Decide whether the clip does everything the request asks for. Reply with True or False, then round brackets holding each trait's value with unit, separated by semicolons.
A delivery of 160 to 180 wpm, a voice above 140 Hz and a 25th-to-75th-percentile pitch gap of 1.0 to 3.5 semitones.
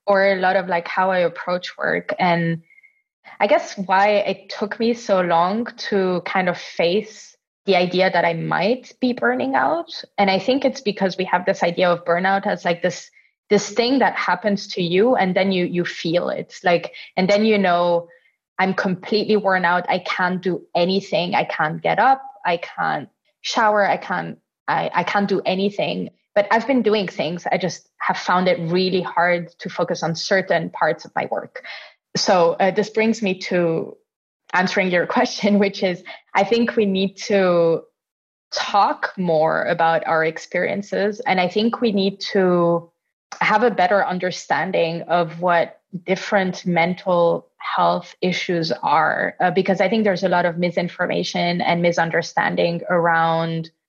True (170 wpm; 185 Hz; 2.8 semitones)